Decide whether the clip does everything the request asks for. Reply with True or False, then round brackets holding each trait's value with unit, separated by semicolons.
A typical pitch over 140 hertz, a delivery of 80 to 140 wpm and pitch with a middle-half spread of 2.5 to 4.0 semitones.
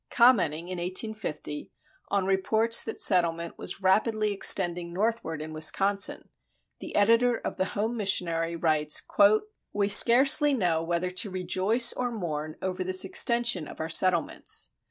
False (185 Hz; 135 wpm; 4.5 semitones)